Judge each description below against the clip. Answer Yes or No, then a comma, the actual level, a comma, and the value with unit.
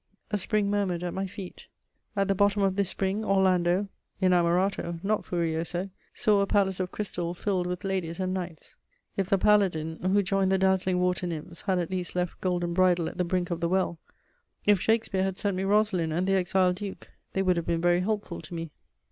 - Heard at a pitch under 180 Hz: No, medium, 185 Hz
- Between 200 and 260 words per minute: Yes, fast, 205 wpm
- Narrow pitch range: Yes, narrow, 2.0 semitones